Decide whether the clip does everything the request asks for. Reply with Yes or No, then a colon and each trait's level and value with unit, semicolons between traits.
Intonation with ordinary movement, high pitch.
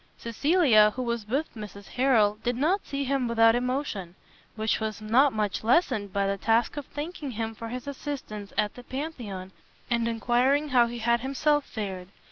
Yes: average, 4.2 semitones; high, 235 Hz